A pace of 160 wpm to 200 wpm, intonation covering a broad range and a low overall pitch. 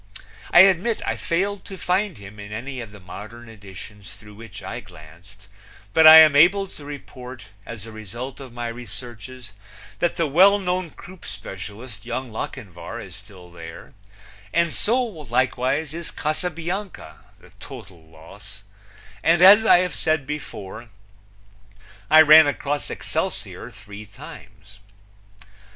No: slow, 135 wpm; wide, 8.0 semitones; low, 125 Hz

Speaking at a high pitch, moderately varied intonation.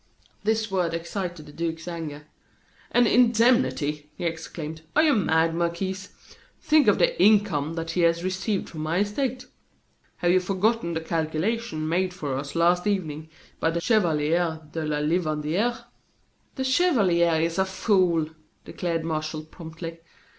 No: medium, 170 Hz; average, 4.1 semitones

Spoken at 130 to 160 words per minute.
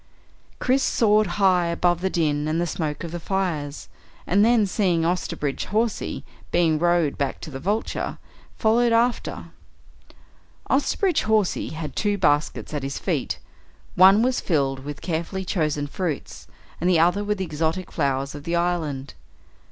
Yes: average, 150 wpm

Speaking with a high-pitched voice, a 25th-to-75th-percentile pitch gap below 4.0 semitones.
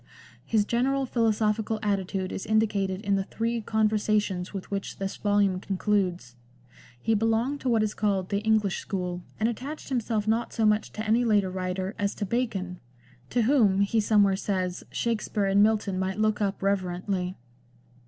Yes: high, 205 Hz; narrow, 2.5 semitones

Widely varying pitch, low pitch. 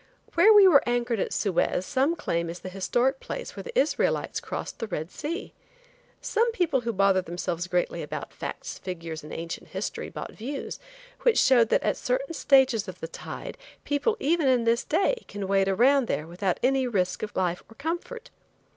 No: wide, 8.0 semitones; high, 235 Hz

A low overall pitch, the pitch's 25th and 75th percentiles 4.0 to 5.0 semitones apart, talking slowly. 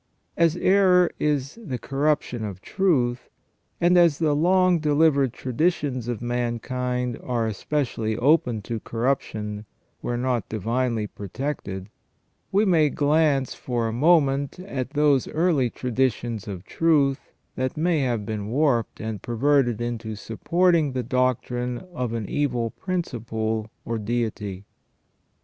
Yes: low, 125 Hz; average, 4.7 semitones; slow, 125 wpm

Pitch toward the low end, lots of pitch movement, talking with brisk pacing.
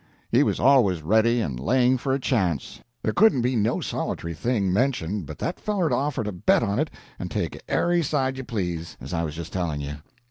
Yes: low, 110 Hz; wide, 7.8 semitones; fast, 210 wpm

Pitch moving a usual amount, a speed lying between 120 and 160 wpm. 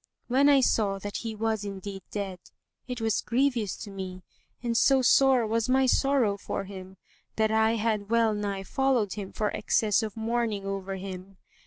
No: average, 3.0 semitones; average, 175 wpm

